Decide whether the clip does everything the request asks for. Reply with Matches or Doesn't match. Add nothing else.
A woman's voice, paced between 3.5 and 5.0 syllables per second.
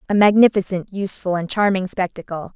Doesn't match